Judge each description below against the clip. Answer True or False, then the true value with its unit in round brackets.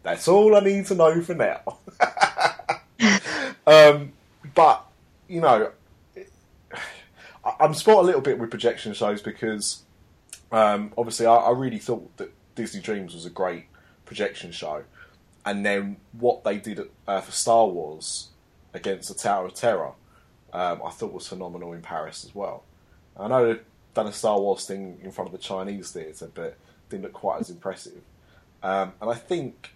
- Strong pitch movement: True (8.6 semitones)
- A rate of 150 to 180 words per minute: True (165 wpm)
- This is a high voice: False (115 Hz)